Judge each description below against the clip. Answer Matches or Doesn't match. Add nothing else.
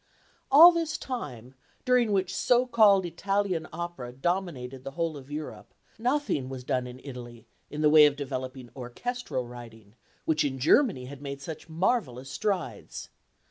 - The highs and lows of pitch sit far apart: Matches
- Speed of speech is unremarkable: Matches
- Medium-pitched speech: Matches